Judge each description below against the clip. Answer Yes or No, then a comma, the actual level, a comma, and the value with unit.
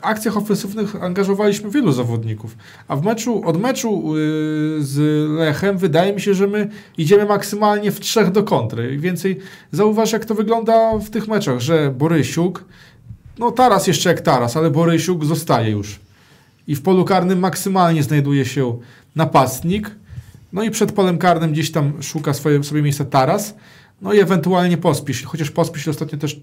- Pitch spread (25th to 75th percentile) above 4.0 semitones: Yes, average, 5.2 semitones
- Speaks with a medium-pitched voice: Yes, medium, 170 Hz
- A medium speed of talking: No, fast, 165 wpm